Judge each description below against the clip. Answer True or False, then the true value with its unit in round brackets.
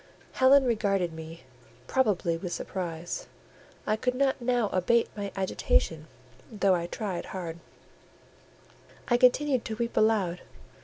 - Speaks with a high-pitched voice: True (200 Hz)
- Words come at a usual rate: False (120 wpm)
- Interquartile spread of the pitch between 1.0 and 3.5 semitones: False (5.6 semitones)